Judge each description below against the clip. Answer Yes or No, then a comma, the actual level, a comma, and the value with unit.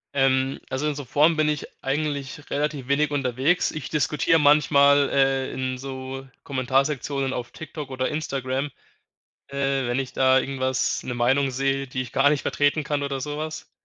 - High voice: No, low, 135 Hz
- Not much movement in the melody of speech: Yes, narrow, 1.9 semitones